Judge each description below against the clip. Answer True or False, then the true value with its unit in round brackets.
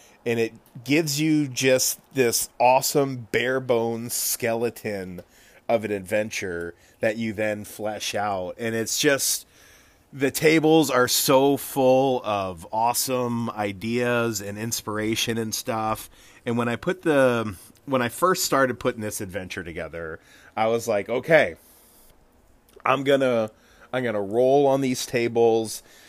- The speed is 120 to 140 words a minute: True (135 wpm)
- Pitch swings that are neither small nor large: True (3.4 semitones)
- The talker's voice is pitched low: True (120 Hz)